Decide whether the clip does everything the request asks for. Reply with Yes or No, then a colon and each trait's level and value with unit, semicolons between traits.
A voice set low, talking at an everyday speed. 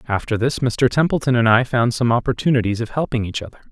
No: low, 120 Hz; fast, 210 wpm